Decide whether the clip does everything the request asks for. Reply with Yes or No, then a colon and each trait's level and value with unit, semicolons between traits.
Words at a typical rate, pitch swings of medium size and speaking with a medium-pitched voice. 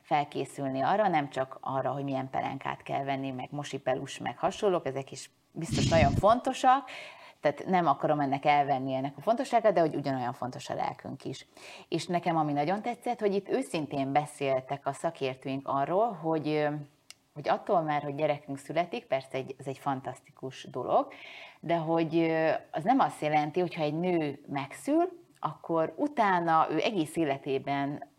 No: fast, 160 wpm; average, 4.0 semitones; medium, 150 Hz